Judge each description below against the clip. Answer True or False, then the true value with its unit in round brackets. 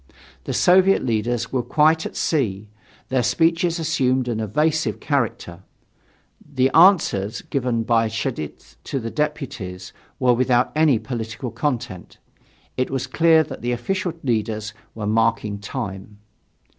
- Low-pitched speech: True (125 Hz)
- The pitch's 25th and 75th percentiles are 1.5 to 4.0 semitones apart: False (5.5 semitones)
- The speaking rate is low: True (130 wpm)